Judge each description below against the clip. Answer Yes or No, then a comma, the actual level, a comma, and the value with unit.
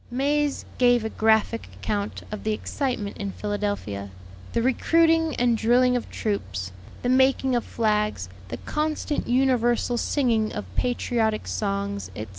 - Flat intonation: No, average, 3.6 semitones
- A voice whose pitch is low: No, high, 230 Hz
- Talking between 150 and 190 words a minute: No, slow, 135 wpm